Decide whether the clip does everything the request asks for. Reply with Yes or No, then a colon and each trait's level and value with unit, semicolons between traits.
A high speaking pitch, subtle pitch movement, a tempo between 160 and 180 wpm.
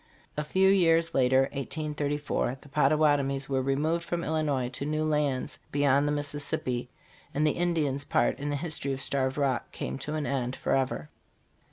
No: medium, 145 Hz; narrow, 2.3 semitones; average, 165 wpm